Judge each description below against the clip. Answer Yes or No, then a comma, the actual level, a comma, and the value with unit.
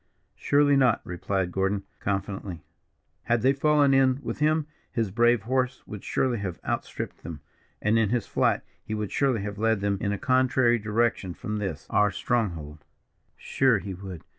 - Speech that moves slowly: No, average, 165 wpm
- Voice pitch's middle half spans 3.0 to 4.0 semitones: No, average, 4.6 semitones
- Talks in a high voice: No, low, 110 Hz